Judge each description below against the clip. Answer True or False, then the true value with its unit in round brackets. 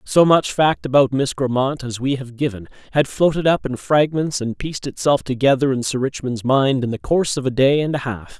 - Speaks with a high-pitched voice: False (135 Hz)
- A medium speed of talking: False (230 wpm)